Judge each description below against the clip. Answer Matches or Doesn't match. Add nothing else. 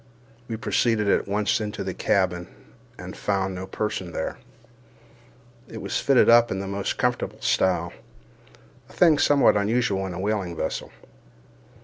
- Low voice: Matches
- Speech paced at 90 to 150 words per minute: Matches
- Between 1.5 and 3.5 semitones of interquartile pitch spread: Matches